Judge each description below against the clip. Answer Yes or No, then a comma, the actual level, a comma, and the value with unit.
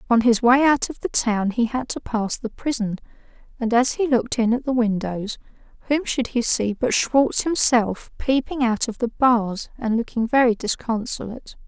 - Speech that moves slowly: No, average, 190 wpm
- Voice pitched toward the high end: Yes, high, 240 Hz